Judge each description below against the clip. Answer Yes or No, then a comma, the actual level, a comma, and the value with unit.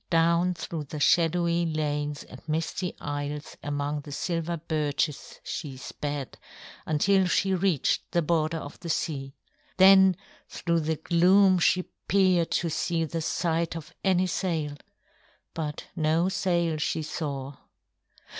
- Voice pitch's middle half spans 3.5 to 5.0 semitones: No, average, 2.8 semitones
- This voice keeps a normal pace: No, slow, 130 wpm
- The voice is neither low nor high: Yes, medium, 165 Hz